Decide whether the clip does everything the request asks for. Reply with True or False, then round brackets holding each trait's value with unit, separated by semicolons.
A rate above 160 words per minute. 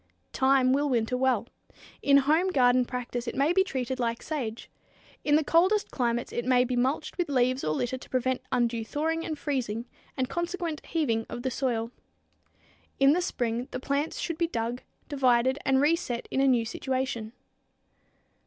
True (170 wpm)